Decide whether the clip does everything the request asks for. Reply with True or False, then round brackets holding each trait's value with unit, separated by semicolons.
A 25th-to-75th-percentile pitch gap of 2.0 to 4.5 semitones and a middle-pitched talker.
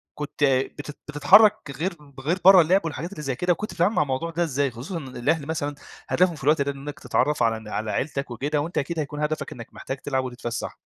True (3.8 semitones; 145 Hz)